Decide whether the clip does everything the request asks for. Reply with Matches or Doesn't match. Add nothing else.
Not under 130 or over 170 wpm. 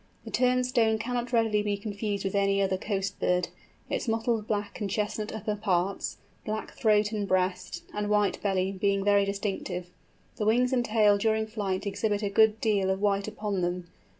Doesn't match